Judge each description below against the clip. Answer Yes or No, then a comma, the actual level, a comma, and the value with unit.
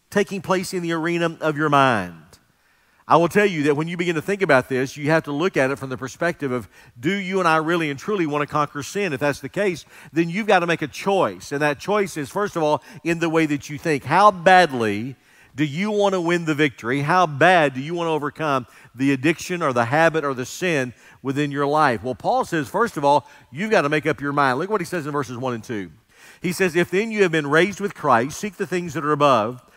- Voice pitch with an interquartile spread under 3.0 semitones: No, average, 4.3 semitones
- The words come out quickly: Yes, fast, 260 wpm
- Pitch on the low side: No, medium, 155 Hz